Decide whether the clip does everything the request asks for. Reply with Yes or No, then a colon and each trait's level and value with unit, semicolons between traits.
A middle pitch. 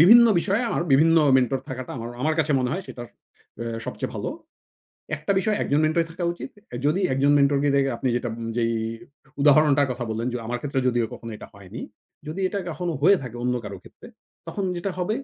Yes: medium, 145 Hz